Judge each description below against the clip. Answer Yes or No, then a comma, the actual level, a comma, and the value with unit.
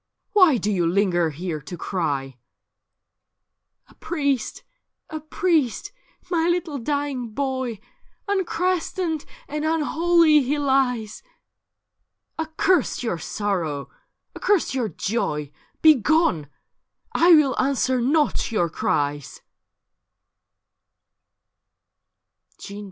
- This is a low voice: No, very high, 265 Hz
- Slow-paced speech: Yes, slow, 95 wpm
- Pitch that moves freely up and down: Yes, wide, 8.8 semitones